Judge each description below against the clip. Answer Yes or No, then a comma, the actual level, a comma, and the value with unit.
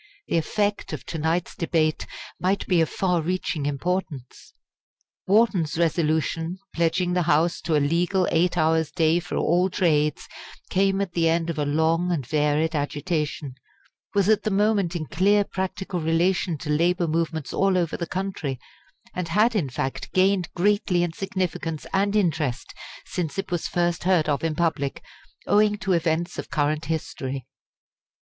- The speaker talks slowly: No, average, 160 wpm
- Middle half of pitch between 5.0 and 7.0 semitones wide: No, average, 3.0 semitones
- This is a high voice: No, medium, 170 Hz